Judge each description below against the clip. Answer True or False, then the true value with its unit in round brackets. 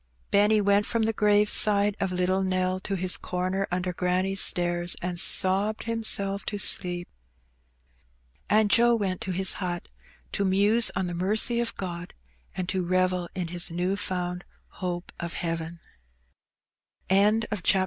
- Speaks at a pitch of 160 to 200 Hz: True (185 Hz)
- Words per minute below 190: True (150 wpm)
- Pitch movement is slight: True (2.3 semitones)